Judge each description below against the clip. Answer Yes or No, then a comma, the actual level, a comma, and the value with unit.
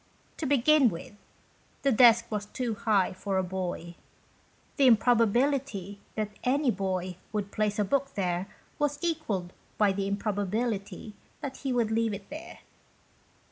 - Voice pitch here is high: Yes, high, 215 Hz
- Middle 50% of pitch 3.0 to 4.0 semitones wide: No, average, 4.4 semitones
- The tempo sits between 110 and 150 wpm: Yes, average, 140 wpm